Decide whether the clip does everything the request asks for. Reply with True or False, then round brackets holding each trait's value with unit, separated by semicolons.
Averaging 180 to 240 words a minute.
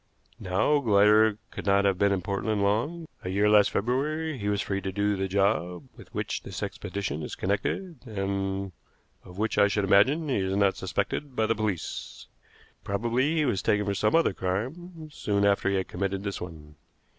True (190 wpm)